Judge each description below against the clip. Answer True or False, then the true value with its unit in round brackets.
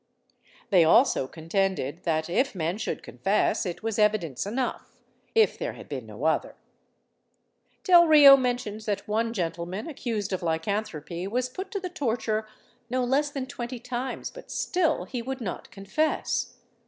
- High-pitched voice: True (215 Hz)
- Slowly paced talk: False (150 wpm)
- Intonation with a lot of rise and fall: True (6.5 semitones)